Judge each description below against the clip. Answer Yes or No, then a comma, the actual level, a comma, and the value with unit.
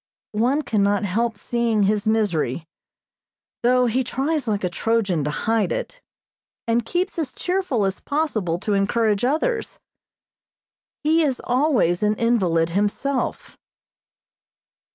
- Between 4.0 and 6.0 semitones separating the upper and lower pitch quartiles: Yes, average, 5.2 semitones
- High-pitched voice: Yes, high, 230 Hz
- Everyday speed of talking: No, slow, 120 wpm